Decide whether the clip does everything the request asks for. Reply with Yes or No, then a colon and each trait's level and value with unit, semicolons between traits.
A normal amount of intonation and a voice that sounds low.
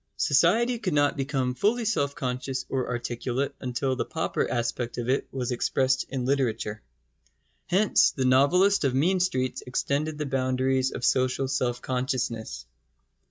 No: narrow, 2.2 semitones; low, 130 Hz